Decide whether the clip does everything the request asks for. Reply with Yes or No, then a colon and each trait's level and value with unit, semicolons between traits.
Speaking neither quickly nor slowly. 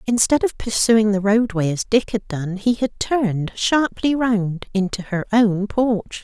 Yes: average, 175 wpm